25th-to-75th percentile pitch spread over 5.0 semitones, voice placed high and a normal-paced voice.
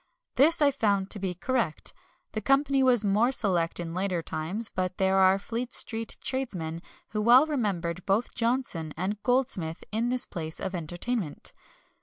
Yes: wide, 5.6 semitones; high, 205 Hz; average, 165 wpm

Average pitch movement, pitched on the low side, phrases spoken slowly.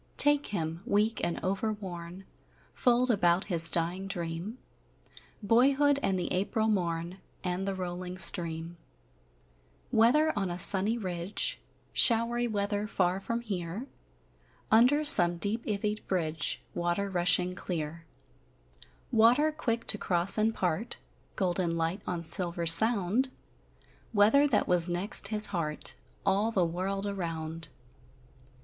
No: average, 4.2 semitones; high, 190 Hz; slow, 120 wpm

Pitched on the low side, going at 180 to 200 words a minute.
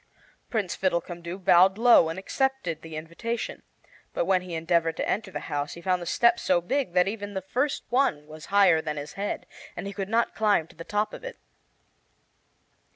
No: medium, 185 Hz; average, 195 wpm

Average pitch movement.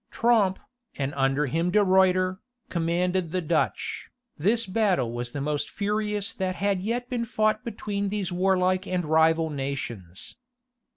Yes: average, 4.4 semitones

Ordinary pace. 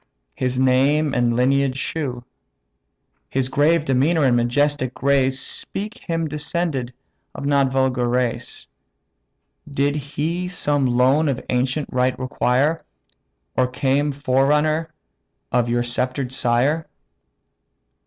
No: slow, 110 wpm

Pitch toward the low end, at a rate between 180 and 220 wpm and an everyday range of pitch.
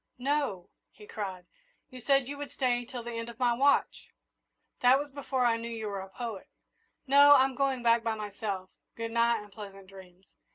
No: high, 235 Hz; average, 195 wpm; average, 4.1 semitones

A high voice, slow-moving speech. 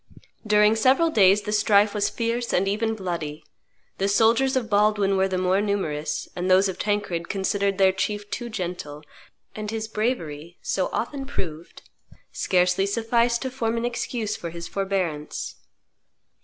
No: high, 205 Hz; average, 155 wpm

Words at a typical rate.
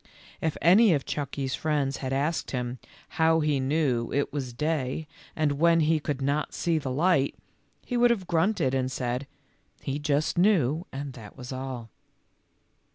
Yes: average, 165 wpm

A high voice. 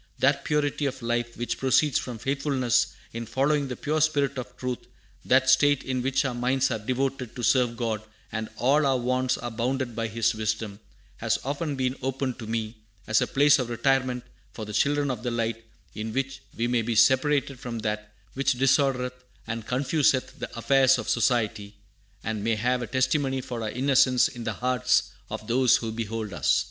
No: low, 125 Hz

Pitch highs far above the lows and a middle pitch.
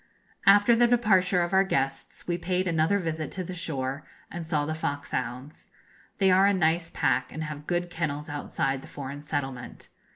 No: average, 4.2 semitones; medium, 165 Hz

